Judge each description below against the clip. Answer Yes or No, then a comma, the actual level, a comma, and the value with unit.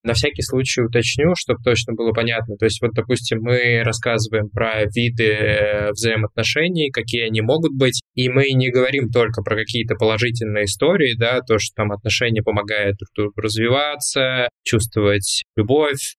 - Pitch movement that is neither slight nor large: No, narrow, 2.2 semitones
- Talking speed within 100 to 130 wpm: No, average, 145 wpm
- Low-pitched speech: Yes, low, 115 Hz